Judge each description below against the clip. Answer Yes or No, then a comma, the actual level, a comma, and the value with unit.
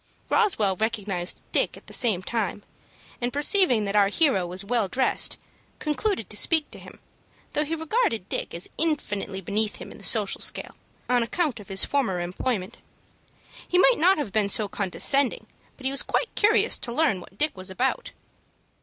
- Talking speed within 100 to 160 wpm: No, average, 175 wpm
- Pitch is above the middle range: Yes, high, 230 Hz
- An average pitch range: No, wide, 7.1 semitones